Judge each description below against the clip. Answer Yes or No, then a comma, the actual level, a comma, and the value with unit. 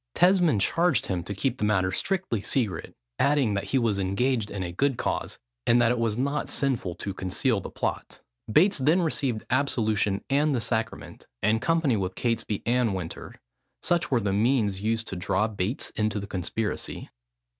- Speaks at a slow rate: No, average, 175 wpm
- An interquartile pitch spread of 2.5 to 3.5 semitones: No, average, 5.2 semitones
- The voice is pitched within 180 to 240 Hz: No, low, 115 Hz